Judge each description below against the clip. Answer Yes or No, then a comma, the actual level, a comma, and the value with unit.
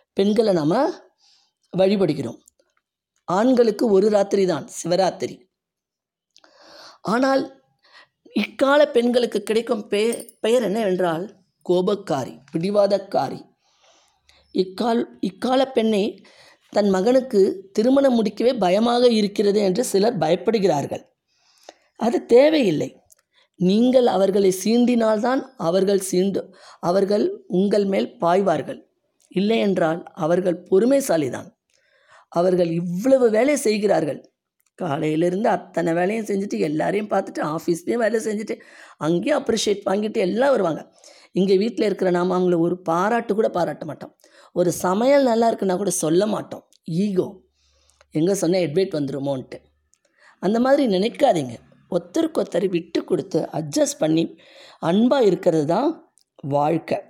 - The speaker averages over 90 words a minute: Yes, average, 100 wpm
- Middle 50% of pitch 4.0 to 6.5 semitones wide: Yes, average, 4.8 semitones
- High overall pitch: Yes, high, 200 Hz